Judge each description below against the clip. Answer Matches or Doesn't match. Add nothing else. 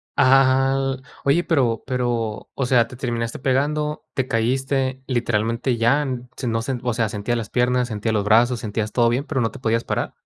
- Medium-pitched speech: Doesn't match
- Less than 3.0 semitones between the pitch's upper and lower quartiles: Matches